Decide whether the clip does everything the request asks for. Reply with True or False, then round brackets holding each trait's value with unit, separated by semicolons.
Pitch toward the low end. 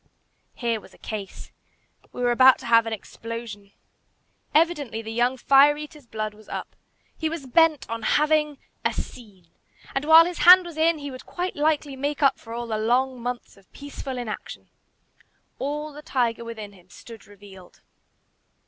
False (250 Hz)